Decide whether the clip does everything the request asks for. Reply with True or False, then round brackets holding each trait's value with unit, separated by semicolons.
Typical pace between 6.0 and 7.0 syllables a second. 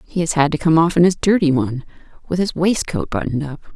True (6.5 syllables/s)